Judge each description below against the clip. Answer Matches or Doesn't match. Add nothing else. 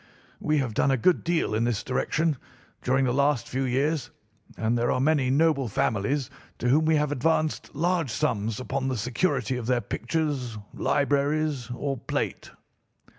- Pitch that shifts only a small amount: Doesn't match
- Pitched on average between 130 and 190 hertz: Matches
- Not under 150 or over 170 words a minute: Matches